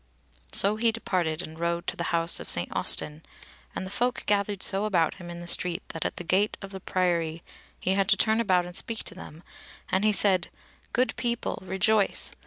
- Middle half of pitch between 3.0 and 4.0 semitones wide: Yes, average, 3.3 semitones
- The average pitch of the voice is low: No, high, 190 Hz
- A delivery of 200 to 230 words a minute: Yes, fast, 205 wpm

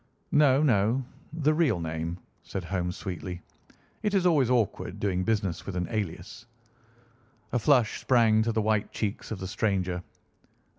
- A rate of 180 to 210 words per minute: No, average, 150 wpm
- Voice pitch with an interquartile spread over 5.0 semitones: Yes, wide, 5.4 semitones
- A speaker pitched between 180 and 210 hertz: No, low, 105 Hz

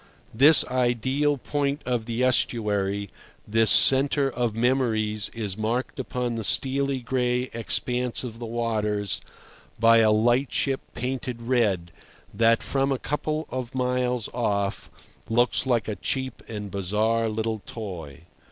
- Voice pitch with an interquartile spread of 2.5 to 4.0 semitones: Yes, average, 3.0 semitones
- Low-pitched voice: Yes, low, 120 Hz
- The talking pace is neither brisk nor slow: No, slow, 130 wpm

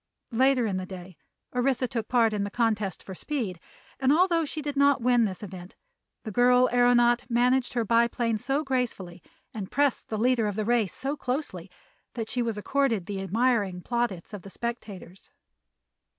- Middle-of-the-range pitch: No, high, 235 Hz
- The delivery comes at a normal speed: Yes, average, 175 wpm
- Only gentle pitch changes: No, average, 3.9 semitones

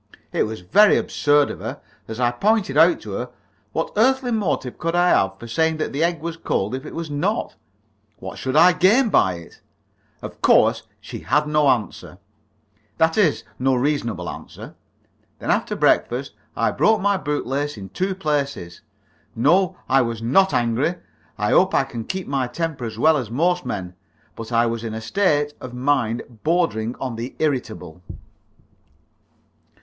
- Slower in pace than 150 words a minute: No, average, 175 wpm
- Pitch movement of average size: No, wide, 6.4 semitones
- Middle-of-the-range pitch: Yes, medium, 145 Hz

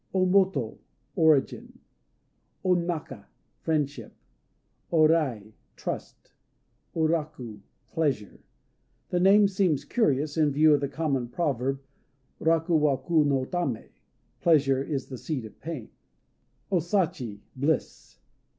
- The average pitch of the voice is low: No, medium, 150 Hz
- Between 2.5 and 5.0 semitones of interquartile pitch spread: Yes, average, 3.9 semitones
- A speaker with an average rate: No, slow, 115 wpm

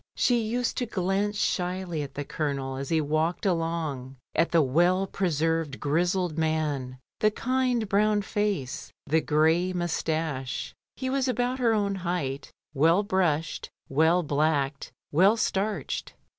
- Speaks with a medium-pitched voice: Yes, medium, 170 Hz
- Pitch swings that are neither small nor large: Yes, average, 4.9 semitones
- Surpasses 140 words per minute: No, slow, 135 wpm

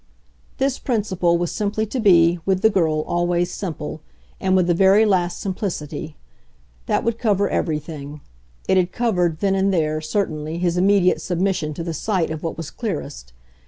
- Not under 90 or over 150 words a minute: No, average, 165 wpm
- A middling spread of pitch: Yes, average, 3.6 semitones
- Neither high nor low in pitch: Yes, medium, 180 Hz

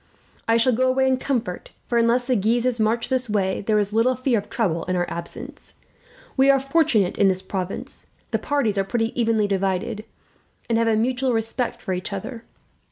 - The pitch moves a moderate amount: Yes, average, 4.1 semitones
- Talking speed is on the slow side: No, average, 195 wpm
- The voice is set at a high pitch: Yes, high, 225 Hz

